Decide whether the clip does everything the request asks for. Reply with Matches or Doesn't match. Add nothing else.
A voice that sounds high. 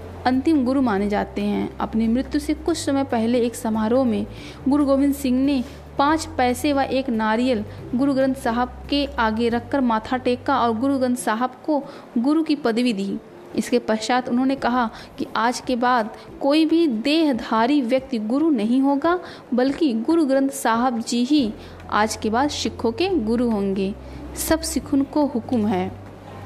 Matches